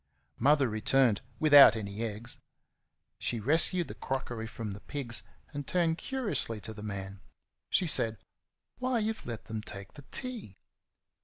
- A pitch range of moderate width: No, wide, 6.6 semitones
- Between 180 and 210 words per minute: No, average, 145 wpm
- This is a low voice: Yes, low, 120 Hz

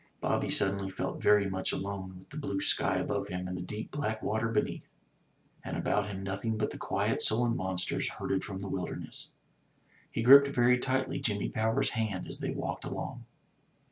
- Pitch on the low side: Yes, low, 105 Hz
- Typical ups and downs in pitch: Yes, average, 3.0 semitones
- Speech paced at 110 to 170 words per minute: No, average, 180 wpm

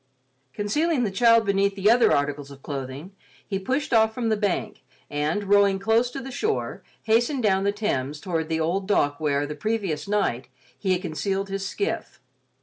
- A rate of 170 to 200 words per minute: Yes, average, 180 wpm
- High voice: Yes, high, 195 Hz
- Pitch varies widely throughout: Yes, wide, 6.1 semitones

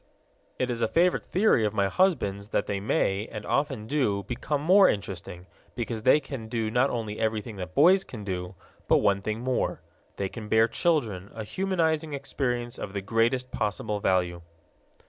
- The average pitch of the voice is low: Yes, low, 110 Hz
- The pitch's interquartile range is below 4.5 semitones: No, average, 5.2 semitones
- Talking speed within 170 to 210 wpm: Yes, average, 175 wpm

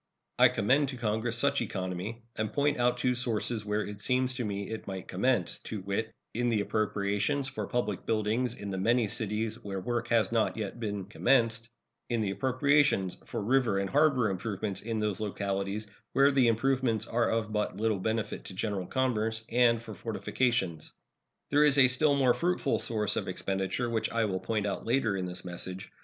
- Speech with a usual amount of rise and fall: Yes, average, 3.5 semitones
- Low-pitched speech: Yes, low, 110 Hz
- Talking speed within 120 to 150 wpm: No, average, 185 wpm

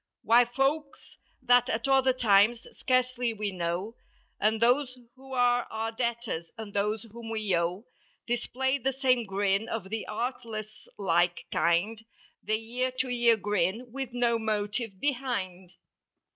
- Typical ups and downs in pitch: Yes, average, 3.3 semitones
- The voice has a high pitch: Yes, high, 230 Hz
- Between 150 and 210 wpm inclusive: No, slow, 135 wpm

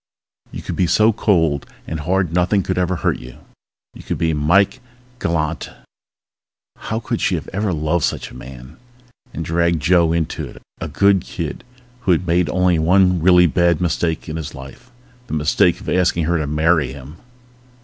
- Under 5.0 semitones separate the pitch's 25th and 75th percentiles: Yes, average, 2.8 semitones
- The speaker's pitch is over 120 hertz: No, very low, 85 Hz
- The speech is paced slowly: No, average, 175 wpm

